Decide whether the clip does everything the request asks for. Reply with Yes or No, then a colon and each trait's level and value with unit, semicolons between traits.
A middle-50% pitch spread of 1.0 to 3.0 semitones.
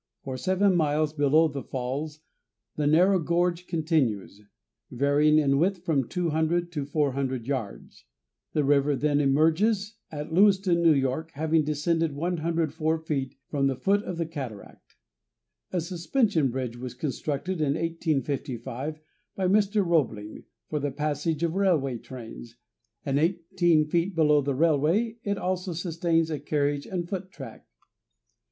No: average, 3.6 semitones